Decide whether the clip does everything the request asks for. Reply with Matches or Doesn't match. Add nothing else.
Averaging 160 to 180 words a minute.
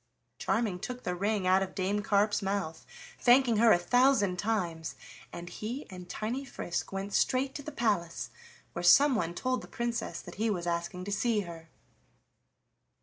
Matches